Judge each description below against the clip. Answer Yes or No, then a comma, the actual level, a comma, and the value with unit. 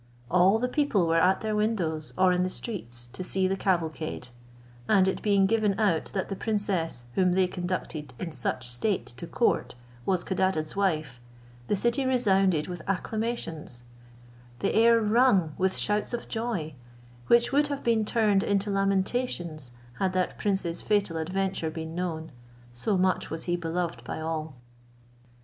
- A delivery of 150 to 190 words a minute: Yes, average, 160 wpm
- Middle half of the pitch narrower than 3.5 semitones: No, average, 4.4 semitones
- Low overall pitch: No, medium, 185 Hz